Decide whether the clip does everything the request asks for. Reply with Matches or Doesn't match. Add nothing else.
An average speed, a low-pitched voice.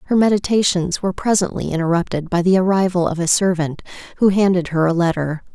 Doesn't match